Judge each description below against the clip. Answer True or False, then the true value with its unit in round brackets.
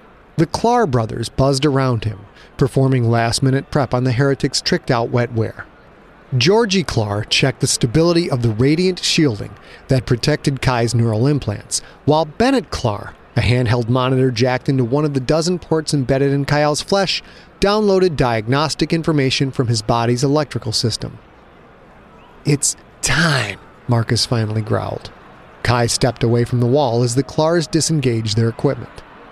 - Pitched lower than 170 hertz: True (135 Hz)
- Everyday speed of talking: True (145 wpm)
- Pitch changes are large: False (4.1 semitones)